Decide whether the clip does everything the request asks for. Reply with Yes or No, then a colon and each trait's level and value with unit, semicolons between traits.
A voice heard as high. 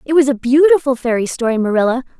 Yes: very high, 260 Hz